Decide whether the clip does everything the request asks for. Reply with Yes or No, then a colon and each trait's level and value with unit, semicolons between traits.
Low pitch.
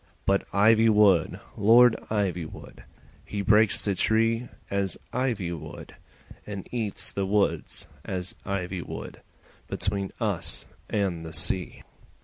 Yes: low, 100 Hz